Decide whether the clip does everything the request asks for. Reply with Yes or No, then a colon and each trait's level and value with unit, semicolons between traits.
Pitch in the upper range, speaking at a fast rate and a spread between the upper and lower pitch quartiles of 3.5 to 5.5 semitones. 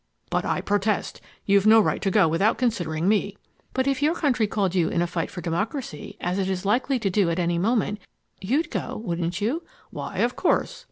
Yes: high, 200 Hz; fast, 210 wpm; average, 4.4 semitones